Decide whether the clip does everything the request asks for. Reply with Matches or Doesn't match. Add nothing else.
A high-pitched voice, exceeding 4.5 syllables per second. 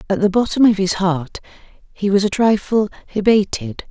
Matches